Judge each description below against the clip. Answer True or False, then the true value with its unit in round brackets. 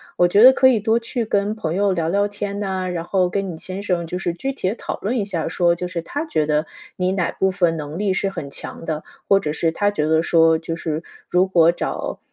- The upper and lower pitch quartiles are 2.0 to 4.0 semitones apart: True (3.5 semitones)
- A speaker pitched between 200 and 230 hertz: False (185 Hz)